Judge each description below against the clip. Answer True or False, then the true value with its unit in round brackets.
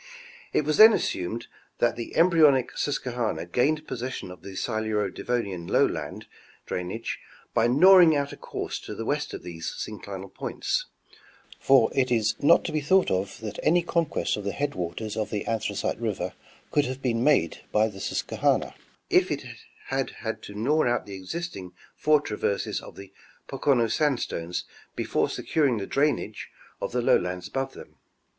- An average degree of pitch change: False (6.4 semitones)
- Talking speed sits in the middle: True (165 wpm)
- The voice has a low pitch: True (120 Hz)